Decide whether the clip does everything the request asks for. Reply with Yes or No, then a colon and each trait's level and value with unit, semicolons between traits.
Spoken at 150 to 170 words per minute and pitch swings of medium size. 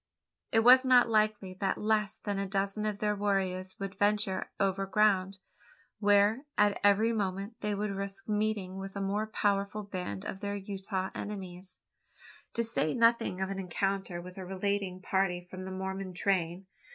No: average, 165 wpm; narrow, 1.8 semitones